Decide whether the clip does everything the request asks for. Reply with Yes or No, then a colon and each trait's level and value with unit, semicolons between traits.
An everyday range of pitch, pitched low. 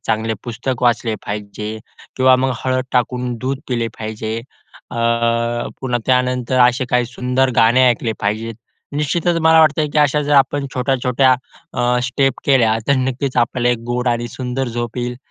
No: narrow, 2.0 semitones; low, 125 Hz